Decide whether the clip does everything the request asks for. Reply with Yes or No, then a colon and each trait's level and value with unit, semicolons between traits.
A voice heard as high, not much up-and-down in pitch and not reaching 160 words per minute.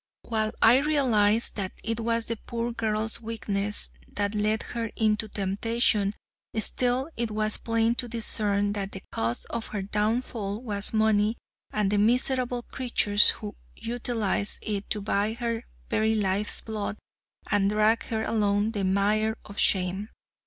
Yes: high, 215 Hz; narrow, 2.1 semitones; average, 145 wpm